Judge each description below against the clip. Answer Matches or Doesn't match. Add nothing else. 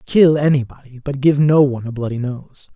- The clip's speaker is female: Doesn't match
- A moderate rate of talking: Matches